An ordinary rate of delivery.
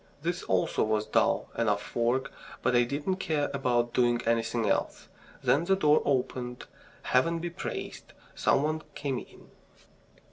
Yes: average, 145 wpm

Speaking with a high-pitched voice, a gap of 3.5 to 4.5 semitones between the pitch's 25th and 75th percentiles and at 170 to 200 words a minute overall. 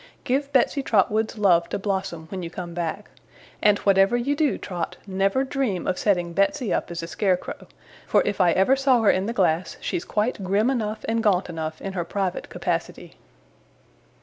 Yes: high, 195 Hz; average, 3.9 semitones; average, 185 wpm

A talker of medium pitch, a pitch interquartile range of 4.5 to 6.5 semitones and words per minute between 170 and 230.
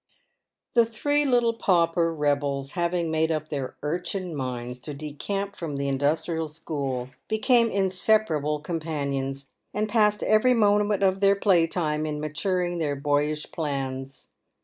No: medium, 160 Hz; wide, 5.5 semitones; slow, 135 wpm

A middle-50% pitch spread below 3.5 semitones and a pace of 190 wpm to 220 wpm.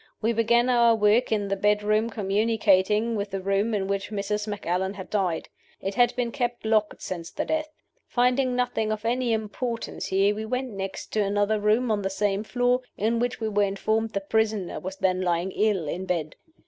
Yes: average, 2.8 semitones; average, 195 wpm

